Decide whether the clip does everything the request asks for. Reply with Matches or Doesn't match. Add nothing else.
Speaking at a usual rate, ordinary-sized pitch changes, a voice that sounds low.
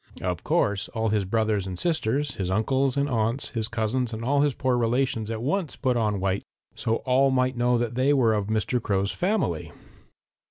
Matches